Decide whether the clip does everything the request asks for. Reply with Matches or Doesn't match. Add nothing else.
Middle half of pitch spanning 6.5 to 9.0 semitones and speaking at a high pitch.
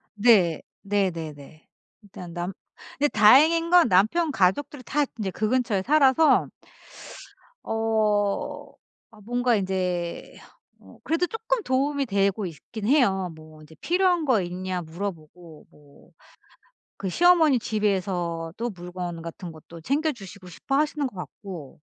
Matches